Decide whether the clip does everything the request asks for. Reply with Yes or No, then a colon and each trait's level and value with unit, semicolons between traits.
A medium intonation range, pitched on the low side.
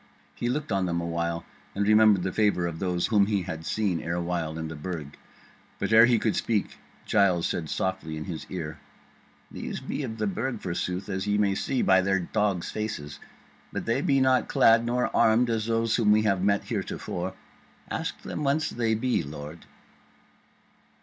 Yes: average, 4.5 semitones; low, 100 Hz